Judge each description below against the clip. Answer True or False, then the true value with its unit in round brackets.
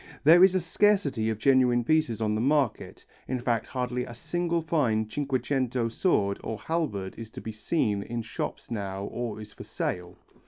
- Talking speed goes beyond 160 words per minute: True (180 wpm)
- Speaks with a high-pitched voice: False (120 Hz)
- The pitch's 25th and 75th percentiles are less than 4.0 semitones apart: False (5.5 semitones)